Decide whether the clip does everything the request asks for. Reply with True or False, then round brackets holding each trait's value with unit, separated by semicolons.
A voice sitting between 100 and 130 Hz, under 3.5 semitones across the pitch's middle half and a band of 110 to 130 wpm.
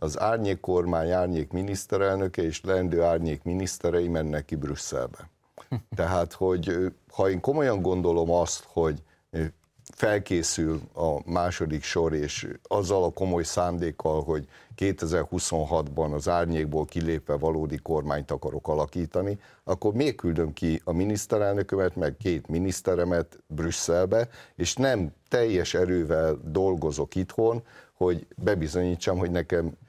False (85 Hz; 2.8 semitones; 115 wpm)